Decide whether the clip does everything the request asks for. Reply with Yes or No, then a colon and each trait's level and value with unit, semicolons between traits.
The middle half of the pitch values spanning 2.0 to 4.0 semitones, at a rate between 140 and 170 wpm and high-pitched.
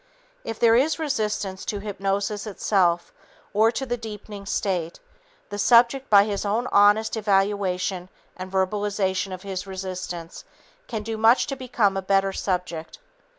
Yes: narrow, 2.5 semitones; average, 145 wpm; high, 200 Hz